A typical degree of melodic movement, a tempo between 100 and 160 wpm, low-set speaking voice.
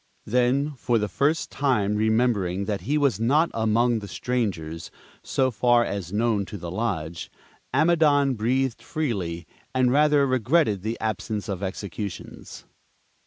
Yes: average, 4.7 semitones; slow, 135 wpm; low, 115 Hz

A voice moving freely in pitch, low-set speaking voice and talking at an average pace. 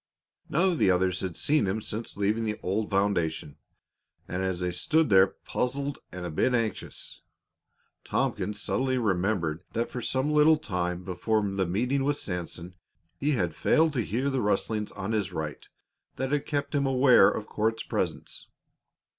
Yes: wide, 6.3 semitones; low, 105 Hz; average, 165 wpm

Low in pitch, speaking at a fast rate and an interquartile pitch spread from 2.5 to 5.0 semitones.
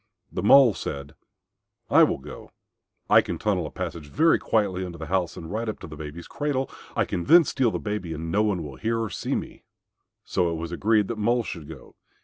No: very low, 95 Hz; fast, 225 wpm; wide, 5.6 semitones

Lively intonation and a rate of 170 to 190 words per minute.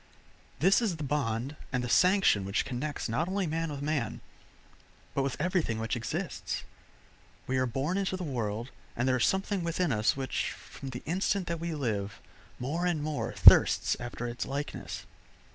Yes: wide, 5.8 semitones; average, 175 wpm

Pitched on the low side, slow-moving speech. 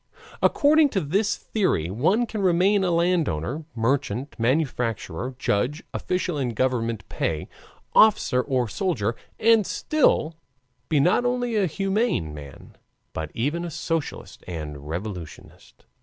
No: medium, 145 Hz; slow, 125 wpm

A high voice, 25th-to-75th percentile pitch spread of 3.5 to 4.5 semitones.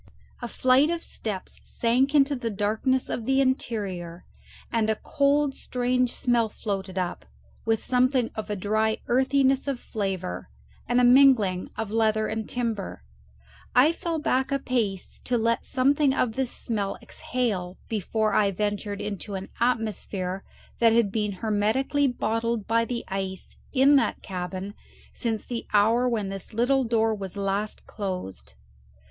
Yes: high, 225 Hz; average, 3.9 semitones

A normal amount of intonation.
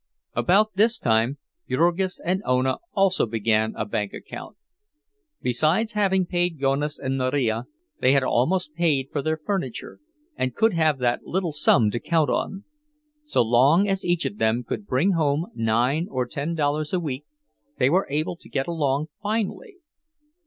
No: wide, 6.2 semitones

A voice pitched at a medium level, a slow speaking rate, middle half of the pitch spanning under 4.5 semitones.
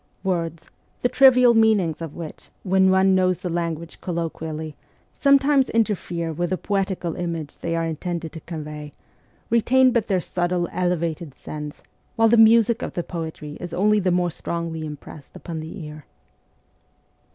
No: medium, 175 Hz; average, 160 wpm; average, 3.8 semitones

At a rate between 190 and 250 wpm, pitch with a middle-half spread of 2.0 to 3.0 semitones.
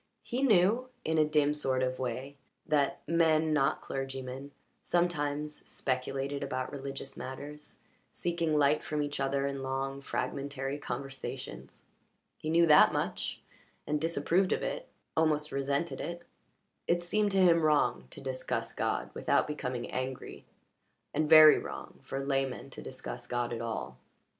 No: average, 145 wpm; average, 2.7 semitones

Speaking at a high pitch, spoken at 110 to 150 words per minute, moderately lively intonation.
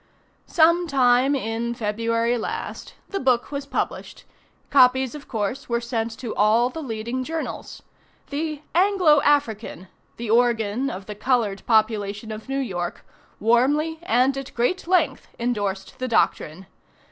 Yes: high, 245 Hz; slow, 135 wpm; average, 4.0 semitones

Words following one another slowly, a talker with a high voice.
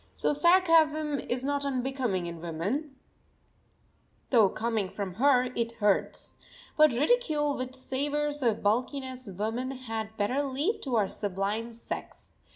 Yes: slow, 130 wpm; very high, 255 Hz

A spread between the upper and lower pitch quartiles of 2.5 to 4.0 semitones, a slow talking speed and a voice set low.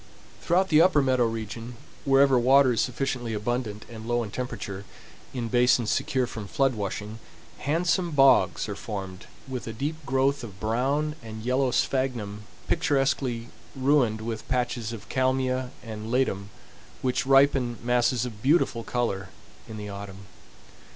No: average, 3.5 semitones; average, 145 wpm; low, 125 Hz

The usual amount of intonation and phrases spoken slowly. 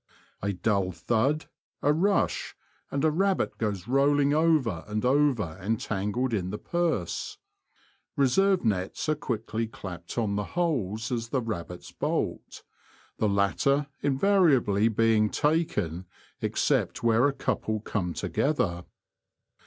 No: wide, 6.2 semitones; slow, 125 wpm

